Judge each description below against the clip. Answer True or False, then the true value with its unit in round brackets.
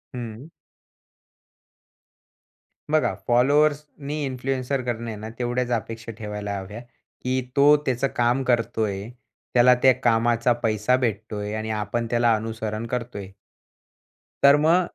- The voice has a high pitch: False (120 Hz)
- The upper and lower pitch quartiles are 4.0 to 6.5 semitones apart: False (2.8 semitones)